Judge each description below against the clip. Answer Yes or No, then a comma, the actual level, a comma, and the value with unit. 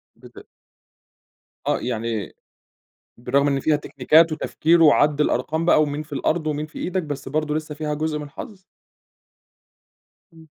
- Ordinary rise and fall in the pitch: No, narrow, 1.7 semitones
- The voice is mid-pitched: Yes, medium, 150 Hz